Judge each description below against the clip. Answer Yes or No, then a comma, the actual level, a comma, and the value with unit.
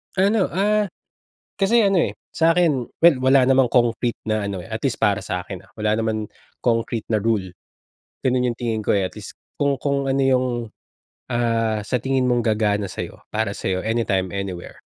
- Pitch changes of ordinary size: Yes, average, 4.0 semitones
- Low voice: Yes, low, 115 Hz